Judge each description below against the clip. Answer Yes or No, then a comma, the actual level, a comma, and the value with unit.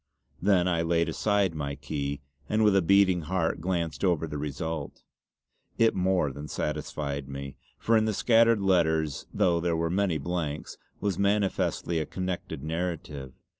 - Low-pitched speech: Yes, very low, 85 Hz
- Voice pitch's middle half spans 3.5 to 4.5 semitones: Yes, average, 4.0 semitones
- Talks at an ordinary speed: Yes, average, 155 wpm